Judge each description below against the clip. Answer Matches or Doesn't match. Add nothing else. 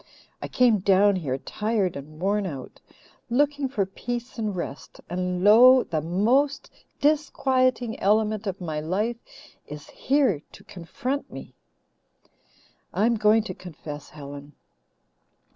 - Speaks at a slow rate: Matches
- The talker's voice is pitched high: Matches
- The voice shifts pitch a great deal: Matches